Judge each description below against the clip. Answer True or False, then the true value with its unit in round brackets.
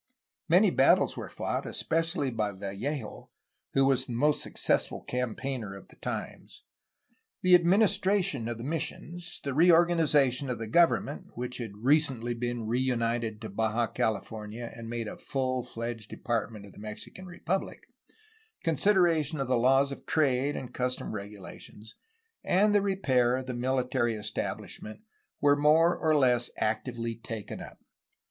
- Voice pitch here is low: True (125 Hz)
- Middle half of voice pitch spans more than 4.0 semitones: True (4.9 semitones)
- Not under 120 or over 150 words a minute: True (145 wpm)